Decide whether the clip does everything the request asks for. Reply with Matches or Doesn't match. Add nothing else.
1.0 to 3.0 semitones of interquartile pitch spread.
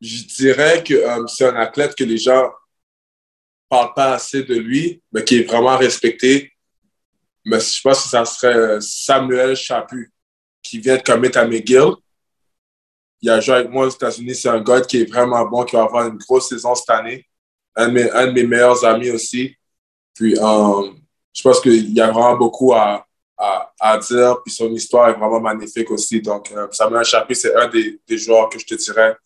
Matches